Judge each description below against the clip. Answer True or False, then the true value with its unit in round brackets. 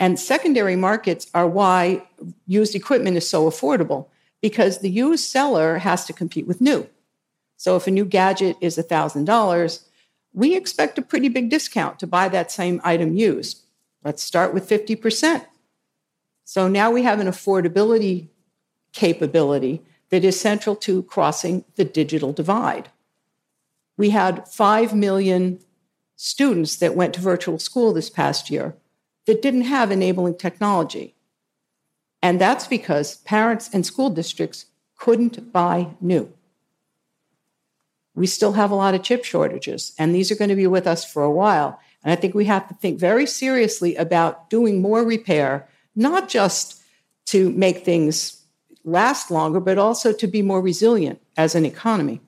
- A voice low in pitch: False (190 Hz)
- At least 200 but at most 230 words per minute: False (155 wpm)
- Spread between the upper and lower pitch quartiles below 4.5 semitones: True (4.1 semitones)